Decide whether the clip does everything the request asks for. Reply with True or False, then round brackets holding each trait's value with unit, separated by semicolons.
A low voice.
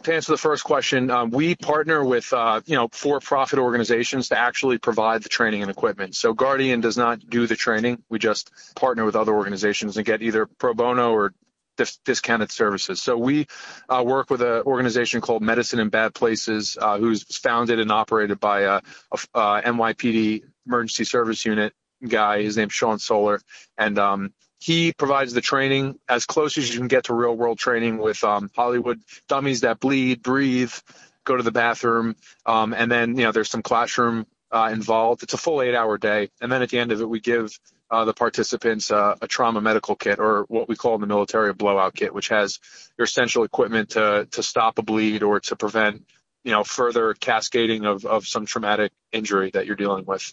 True (115 Hz)